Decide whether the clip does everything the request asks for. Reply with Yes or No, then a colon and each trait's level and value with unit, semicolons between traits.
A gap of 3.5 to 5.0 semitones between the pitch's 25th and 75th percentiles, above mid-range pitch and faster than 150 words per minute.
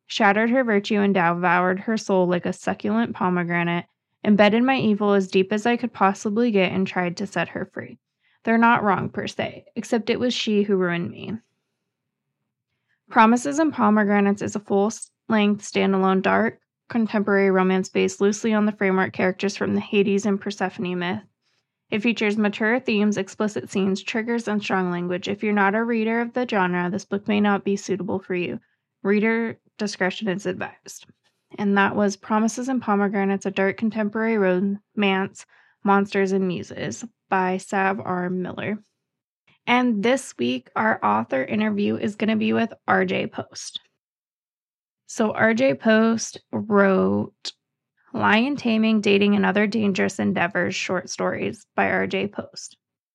No: narrow, 2.6 semitones; high, 200 Hz; average, 160 wpm